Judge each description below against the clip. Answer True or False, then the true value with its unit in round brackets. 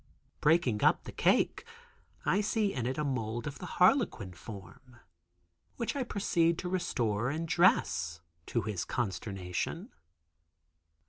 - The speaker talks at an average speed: False (130 wpm)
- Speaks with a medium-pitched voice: False (130 Hz)